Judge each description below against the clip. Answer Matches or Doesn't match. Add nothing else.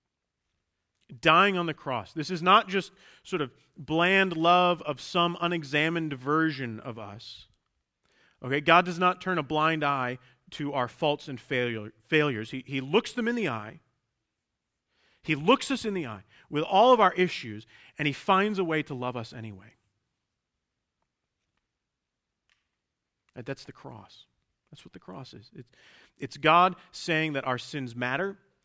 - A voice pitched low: Doesn't match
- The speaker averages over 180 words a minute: Doesn't match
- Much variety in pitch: Matches